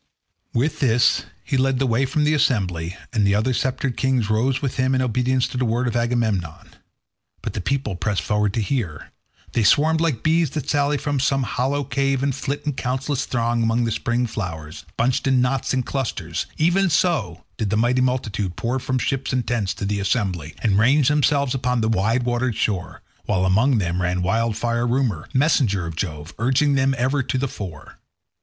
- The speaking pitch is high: No, low, 125 Hz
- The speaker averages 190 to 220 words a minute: Yes, average, 195 wpm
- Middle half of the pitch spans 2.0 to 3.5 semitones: No, average, 4.3 semitones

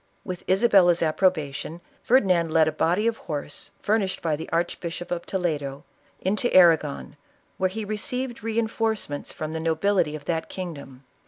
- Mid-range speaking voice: Yes, medium, 175 Hz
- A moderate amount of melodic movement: Yes, average, 4.4 semitones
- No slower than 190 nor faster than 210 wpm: No, average, 160 wpm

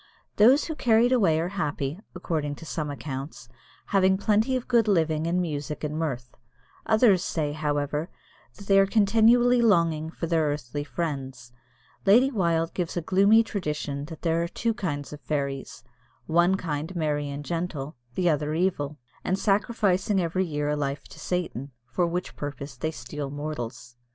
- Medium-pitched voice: Yes, medium, 165 Hz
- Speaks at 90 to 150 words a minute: No, average, 165 wpm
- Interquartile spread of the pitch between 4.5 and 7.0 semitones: Yes, average, 4.9 semitones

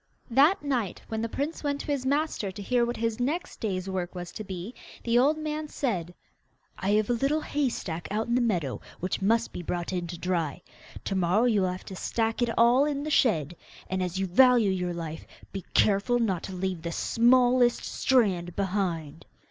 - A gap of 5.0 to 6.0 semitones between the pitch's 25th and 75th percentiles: Yes, wide, 5.6 semitones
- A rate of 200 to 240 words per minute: Yes, fast, 205 wpm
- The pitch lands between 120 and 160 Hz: No, high, 215 Hz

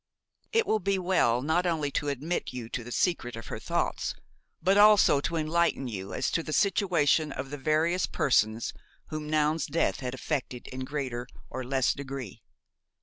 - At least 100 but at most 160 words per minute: No, average, 175 wpm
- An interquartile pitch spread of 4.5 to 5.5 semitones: Yes, average, 4.8 semitones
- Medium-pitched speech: Yes, medium, 145 Hz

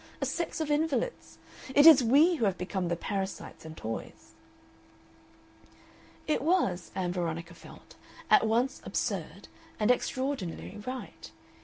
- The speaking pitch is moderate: No, high, 220 Hz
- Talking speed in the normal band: No, slow, 130 wpm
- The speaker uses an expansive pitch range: Yes, wide, 8.3 semitones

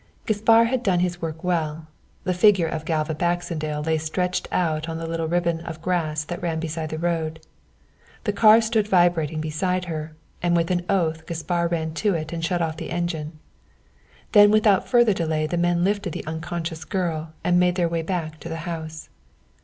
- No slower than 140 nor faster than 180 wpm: No, average, 190 wpm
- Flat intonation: Yes, narrow, 2.1 semitones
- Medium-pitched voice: Yes, medium, 170 Hz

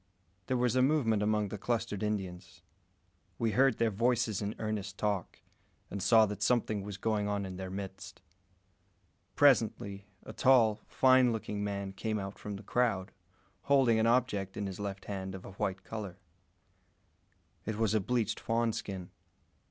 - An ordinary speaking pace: Yes, average, 160 wpm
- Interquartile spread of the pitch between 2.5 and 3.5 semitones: Yes, average, 2.8 semitones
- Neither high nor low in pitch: No, low, 105 Hz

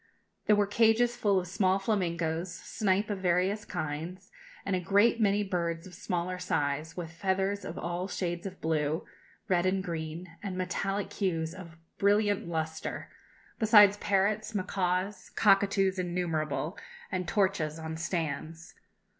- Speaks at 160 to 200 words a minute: No, average, 140 wpm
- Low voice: No, medium, 185 Hz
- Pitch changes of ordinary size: Yes, average, 3.1 semitones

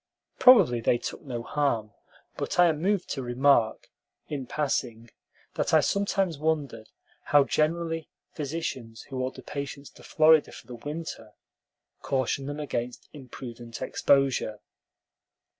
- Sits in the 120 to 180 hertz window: Yes, medium, 140 Hz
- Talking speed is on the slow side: Yes, slow, 125 wpm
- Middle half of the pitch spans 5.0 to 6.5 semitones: No, average, 4.3 semitones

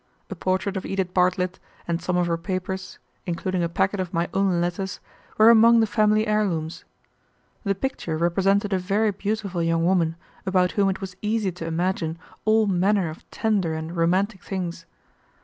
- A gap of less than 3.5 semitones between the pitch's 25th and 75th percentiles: Yes, average, 2.8 semitones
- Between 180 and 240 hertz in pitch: Yes, medium, 185 Hz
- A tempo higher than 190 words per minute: No, average, 170 wpm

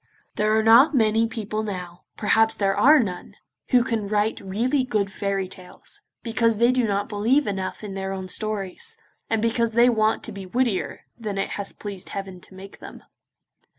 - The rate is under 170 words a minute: No, average, 185 wpm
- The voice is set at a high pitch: Yes, high, 215 Hz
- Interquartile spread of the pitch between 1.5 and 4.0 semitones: Yes, average, 2.8 semitones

